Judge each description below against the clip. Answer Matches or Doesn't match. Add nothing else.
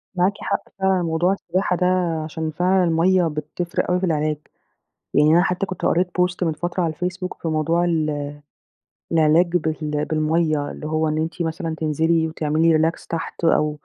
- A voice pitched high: Doesn't match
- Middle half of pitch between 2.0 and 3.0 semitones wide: Matches